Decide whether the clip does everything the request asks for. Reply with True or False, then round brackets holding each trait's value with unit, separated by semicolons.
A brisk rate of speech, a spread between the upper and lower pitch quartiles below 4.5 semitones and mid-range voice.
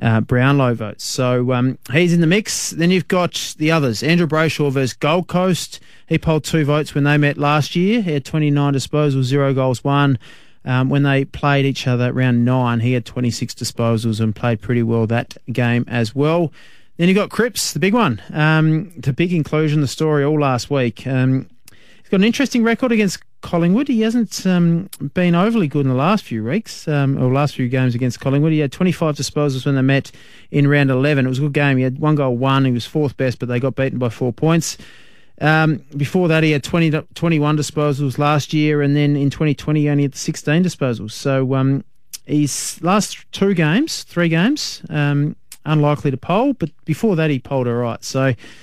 True (210 wpm; 4.0 semitones; 145 Hz)